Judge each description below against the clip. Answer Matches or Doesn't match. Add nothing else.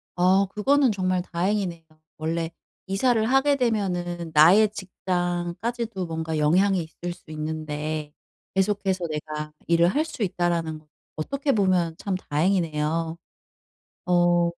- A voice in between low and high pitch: Matches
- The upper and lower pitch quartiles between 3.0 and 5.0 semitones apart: Matches